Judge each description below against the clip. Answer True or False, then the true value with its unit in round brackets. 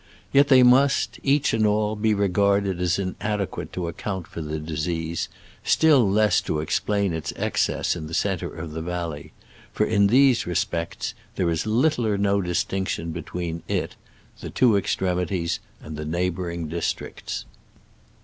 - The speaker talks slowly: False (155 wpm)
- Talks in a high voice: False (95 Hz)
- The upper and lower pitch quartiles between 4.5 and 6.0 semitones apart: False (4.0 semitones)